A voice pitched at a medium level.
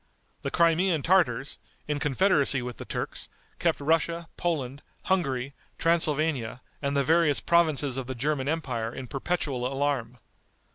Yes: medium, 145 Hz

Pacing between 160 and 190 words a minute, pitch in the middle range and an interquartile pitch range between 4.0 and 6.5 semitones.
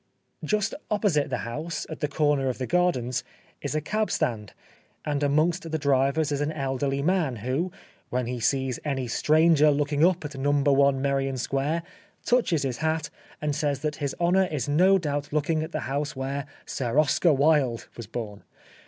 No: average, 185 wpm; medium, 145 Hz; average, 2.9 semitones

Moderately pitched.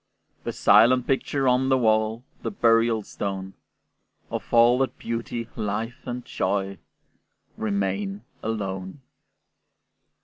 No: low, 115 Hz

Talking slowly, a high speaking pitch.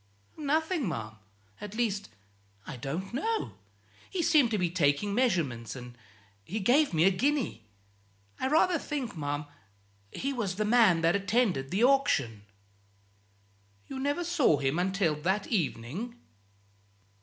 Yes: slow, 130 wpm; high, 200 Hz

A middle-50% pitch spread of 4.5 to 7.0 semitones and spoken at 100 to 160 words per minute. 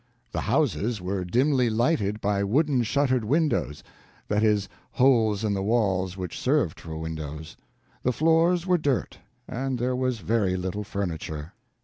Yes: wide, 5.4 semitones; average, 140 wpm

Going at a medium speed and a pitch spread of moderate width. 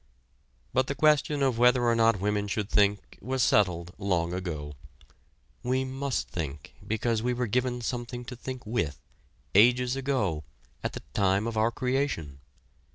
Yes: average, 155 wpm; average, 4.4 semitones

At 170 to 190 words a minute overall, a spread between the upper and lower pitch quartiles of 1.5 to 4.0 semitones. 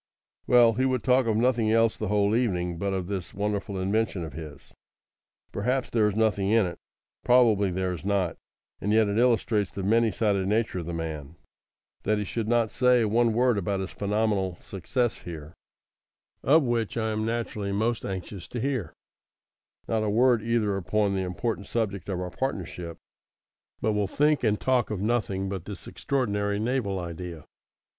Yes: average, 175 wpm; average, 3.4 semitones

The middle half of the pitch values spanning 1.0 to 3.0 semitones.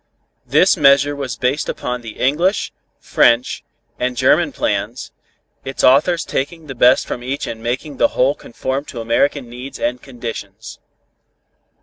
Yes: narrow, 2.6 semitones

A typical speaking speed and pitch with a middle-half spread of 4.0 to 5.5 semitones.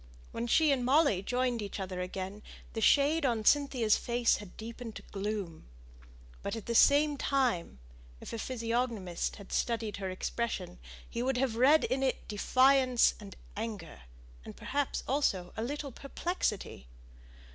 Yes: average, 150 wpm; average, 4.7 semitones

